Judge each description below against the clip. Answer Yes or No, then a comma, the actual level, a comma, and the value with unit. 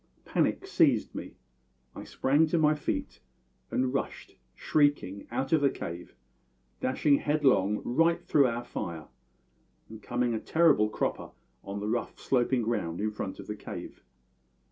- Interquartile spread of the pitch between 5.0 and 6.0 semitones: Yes, wide, 5.4 semitones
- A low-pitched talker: Yes, low, 120 Hz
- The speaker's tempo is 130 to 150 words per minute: Yes, average, 145 wpm